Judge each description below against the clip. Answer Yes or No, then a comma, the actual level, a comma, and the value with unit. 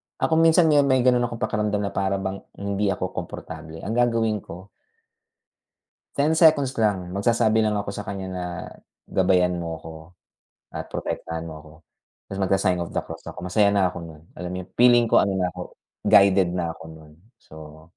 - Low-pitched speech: Yes, very low, 95 Hz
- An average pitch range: Yes, average, 3.7 semitones